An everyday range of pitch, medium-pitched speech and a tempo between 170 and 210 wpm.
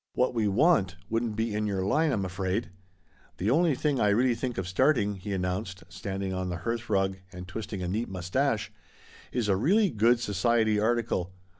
No: average, 3.9 semitones; low, 105 Hz; average, 180 wpm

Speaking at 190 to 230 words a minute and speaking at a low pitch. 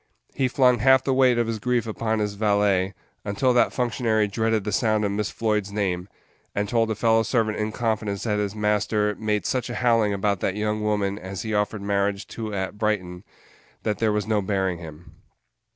Yes: average, 200 wpm; low, 105 Hz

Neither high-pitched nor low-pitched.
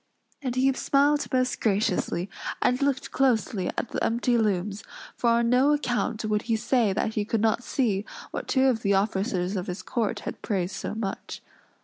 No: high, 225 Hz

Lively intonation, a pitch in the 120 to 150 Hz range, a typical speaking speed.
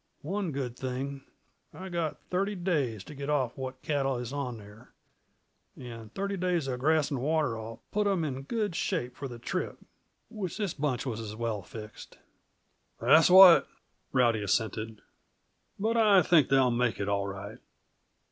Yes: wide, 6.7 semitones; low, 135 Hz; average, 160 wpm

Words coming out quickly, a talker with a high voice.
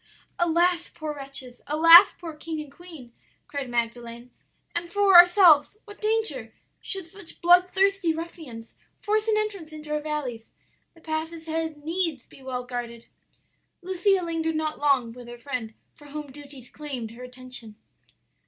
No: average, 145 wpm; very high, 310 Hz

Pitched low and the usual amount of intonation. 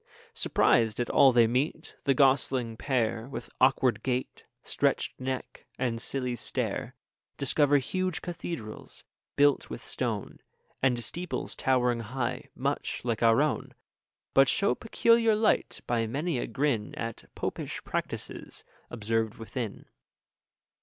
Yes: low, 130 Hz; average, 3.6 semitones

